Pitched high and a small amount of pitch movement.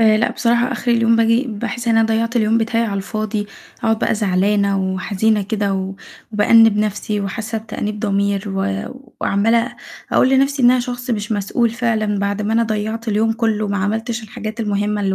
Yes: high, 220 Hz; narrow, 2.0 semitones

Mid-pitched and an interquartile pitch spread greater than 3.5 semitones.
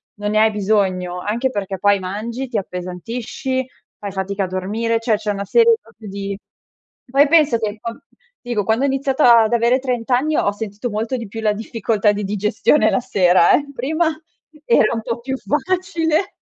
No: high, 225 Hz; average, 4.2 semitones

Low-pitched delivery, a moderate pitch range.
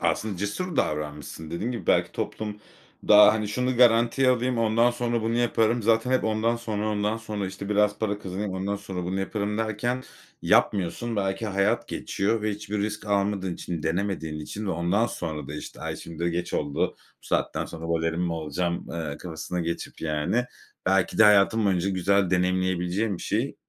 Yes: low, 100 Hz; average, 4.0 semitones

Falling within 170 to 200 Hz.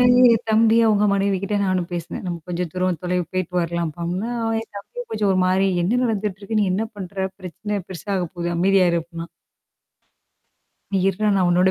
Yes: medium, 185 Hz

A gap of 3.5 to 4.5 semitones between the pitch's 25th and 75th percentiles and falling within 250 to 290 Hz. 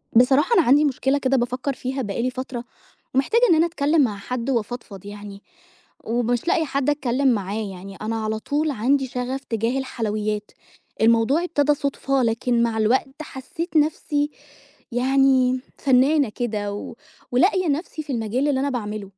Yes: average, 3.9 semitones; very high, 255 Hz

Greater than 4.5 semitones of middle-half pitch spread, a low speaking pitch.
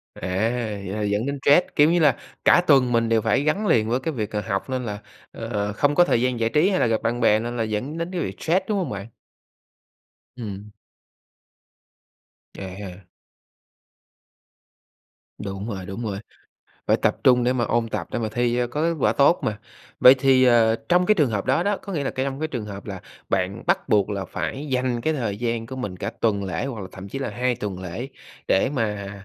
Yes: average, 4.9 semitones; low, 120 Hz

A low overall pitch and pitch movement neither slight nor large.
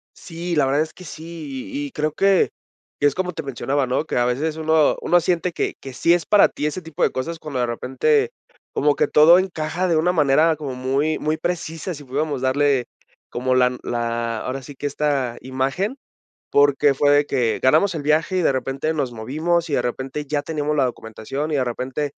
No: medium, 145 Hz; average, 3.7 semitones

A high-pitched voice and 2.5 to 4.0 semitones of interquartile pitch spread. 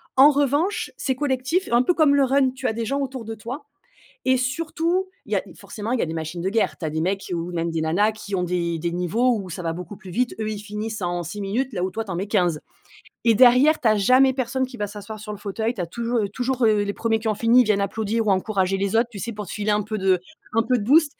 No: high, 215 Hz; average, 4.8 semitones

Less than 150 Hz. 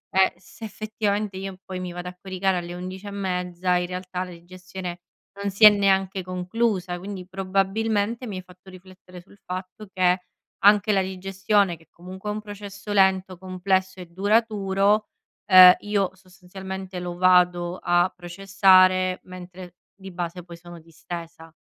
No: medium, 185 Hz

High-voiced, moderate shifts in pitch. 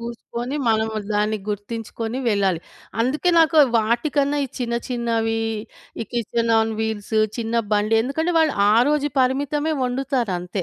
Yes: high, 235 Hz; average, 3.6 semitones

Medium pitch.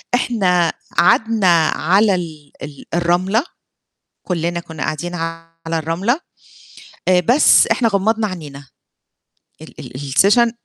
Yes: medium, 175 Hz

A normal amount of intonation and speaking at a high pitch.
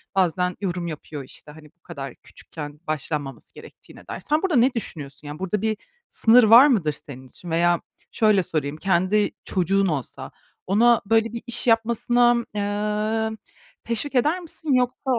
No: wide, 6.7 semitones; high, 205 Hz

